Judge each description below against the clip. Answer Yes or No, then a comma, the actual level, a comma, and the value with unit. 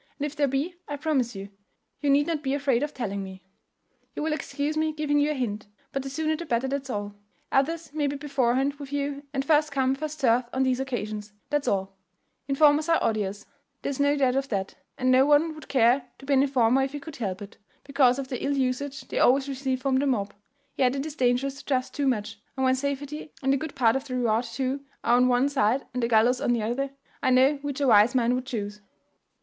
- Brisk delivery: Yes, fast, 240 wpm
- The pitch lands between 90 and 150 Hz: No, very high, 270 Hz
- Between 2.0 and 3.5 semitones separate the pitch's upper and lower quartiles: Yes, average, 2.7 semitones